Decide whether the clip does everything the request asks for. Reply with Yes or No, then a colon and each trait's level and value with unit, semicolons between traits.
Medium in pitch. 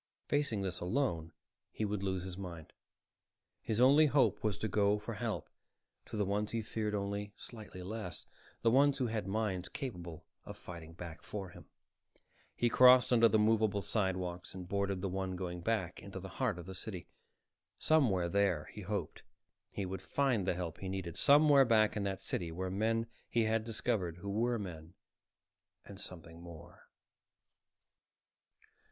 No: low, 100 Hz